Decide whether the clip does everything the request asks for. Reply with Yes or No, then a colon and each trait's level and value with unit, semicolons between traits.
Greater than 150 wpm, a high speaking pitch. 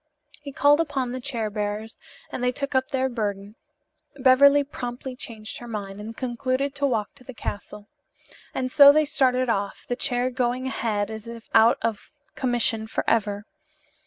Yes: average, 165 wpm; high, 245 Hz